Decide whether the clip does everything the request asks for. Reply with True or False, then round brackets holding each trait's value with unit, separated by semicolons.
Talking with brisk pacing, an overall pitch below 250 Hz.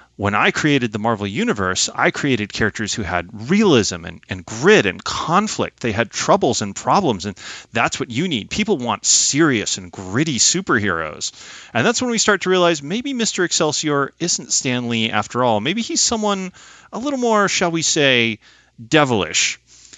False (175 wpm; 140 Hz)